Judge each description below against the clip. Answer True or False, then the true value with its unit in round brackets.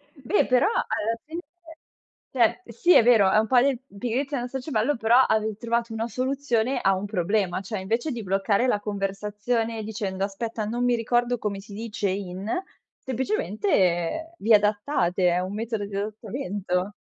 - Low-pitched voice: False (220 Hz)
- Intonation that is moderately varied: True (3.5 semitones)